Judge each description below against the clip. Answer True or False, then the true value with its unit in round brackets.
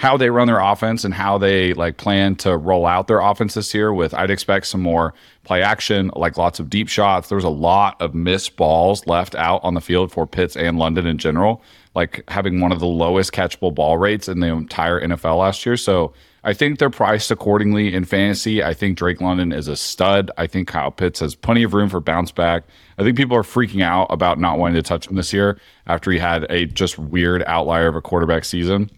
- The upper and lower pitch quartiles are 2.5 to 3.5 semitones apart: True (3.1 semitones)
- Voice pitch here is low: True (90 Hz)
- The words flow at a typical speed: False (230 wpm)